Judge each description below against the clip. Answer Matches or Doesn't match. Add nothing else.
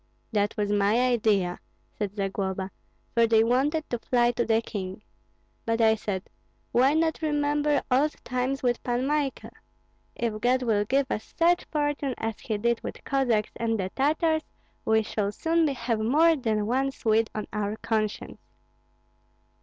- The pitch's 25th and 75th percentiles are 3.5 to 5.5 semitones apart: Matches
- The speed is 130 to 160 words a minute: Matches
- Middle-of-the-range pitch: Doesn't match